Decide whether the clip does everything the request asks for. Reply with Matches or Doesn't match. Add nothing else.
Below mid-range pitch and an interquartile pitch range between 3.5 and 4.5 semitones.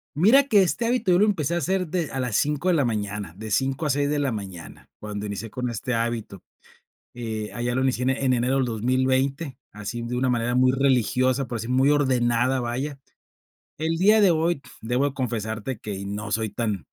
Matches